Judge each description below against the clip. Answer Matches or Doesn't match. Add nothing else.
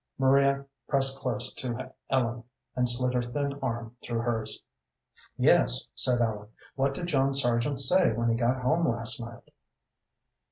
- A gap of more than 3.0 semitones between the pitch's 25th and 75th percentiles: Doesn't match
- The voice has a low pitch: Matches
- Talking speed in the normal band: Matches